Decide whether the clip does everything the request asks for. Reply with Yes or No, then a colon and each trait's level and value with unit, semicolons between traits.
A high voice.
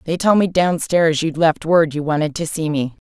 No: medium, 160 Hz